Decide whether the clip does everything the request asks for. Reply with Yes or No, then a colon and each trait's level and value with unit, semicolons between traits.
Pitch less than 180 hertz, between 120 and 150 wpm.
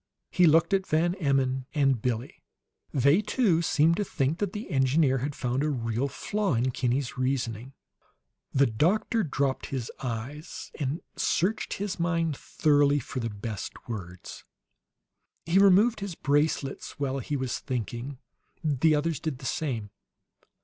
Yes: medium, 140 Hz; average, 145 wpm